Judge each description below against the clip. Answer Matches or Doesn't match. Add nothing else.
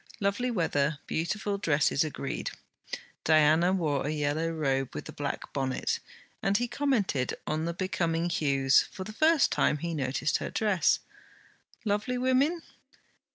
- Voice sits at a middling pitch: Matches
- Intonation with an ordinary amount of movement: Doesn't match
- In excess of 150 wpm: Doesn't match